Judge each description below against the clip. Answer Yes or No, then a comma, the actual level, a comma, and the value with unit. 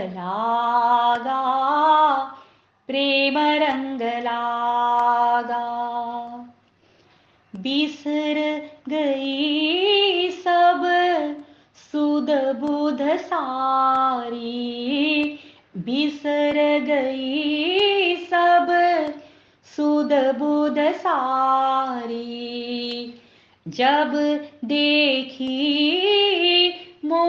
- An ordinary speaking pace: No, slow, 35 wpm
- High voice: Yes, very high, 290 Hz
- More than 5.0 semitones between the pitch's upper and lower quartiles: No, average, 3.5 semitones